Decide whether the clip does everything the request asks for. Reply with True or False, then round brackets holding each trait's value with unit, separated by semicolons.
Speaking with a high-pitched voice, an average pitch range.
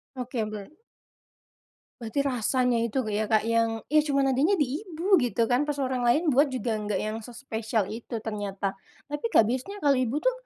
True (250 Hz; 4.3 semitones)